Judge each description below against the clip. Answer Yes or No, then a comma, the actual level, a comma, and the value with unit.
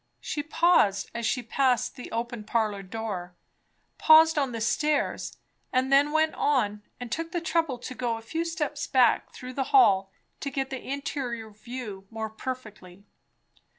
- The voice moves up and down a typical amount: Yes, average, 4.8 semitones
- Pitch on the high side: Yes, very high, 250 Hz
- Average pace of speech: Yes, average, 160 wpm